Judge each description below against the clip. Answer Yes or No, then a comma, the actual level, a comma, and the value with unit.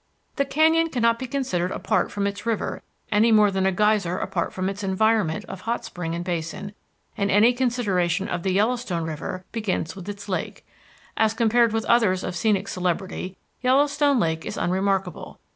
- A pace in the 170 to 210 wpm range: Yes, average, 175 wpm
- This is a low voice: No, high, 200 Hz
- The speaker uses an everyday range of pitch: Yes, average, 4.0 semitones